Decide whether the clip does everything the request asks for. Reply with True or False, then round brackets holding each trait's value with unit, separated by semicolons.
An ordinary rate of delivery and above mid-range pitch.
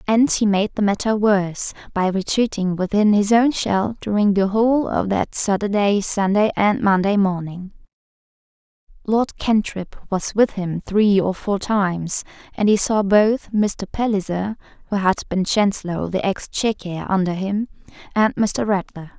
True (155 wpm; 200 Hz)